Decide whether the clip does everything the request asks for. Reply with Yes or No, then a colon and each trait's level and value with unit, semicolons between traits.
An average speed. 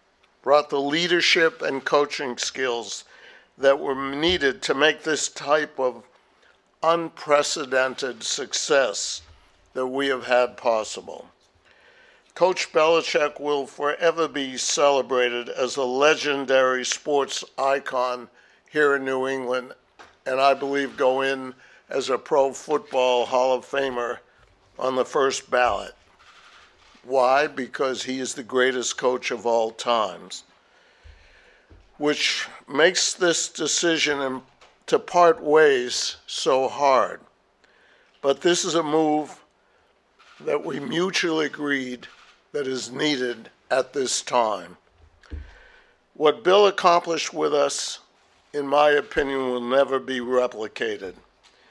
No: slow, 115 wpm